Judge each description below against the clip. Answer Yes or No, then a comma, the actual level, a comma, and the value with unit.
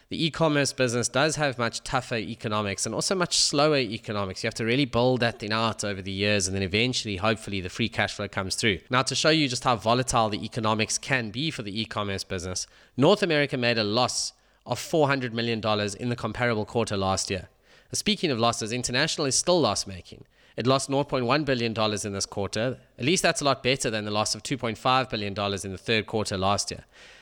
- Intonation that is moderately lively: Yes, average, 4.0 semitones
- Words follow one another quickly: Yes, fast, 215 wpm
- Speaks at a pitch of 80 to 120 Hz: Yes, low, 115 Hz